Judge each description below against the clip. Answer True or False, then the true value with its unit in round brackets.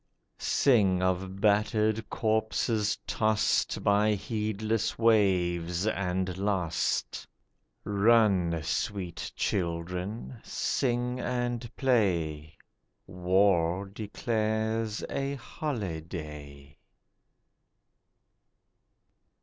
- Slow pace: True (65 wpm)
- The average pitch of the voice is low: True (100 Hz)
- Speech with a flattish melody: False (3.7 semitones)